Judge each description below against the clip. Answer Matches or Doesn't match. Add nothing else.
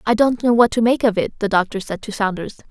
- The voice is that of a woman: Matches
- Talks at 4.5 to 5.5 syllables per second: Doesn't match